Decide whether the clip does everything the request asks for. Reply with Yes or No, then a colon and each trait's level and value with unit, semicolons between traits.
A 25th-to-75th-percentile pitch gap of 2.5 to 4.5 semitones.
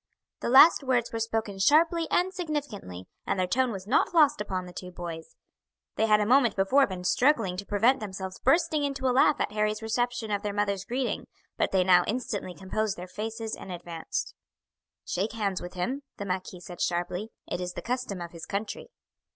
No: average, 5.3 semitones